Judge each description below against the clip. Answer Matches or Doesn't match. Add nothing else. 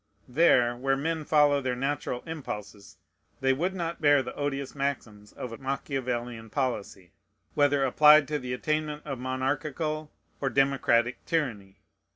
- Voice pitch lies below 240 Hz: Matches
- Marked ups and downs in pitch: Doesn't match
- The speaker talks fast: Doesn't match